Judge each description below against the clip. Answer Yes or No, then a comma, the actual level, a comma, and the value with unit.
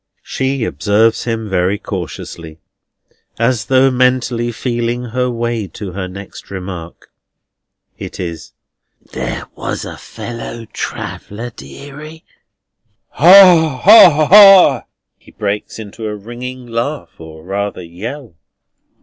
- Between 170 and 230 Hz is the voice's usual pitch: No, low, 115 Hz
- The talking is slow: Yes, slow, 110 wpm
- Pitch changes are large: No, average, 4.6 semitones